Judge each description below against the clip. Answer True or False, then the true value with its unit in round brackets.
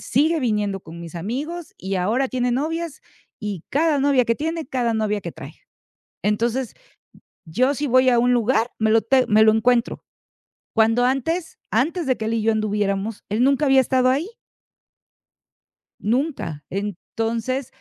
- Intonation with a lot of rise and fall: False (4.0 semitones)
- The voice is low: False (240 Hz)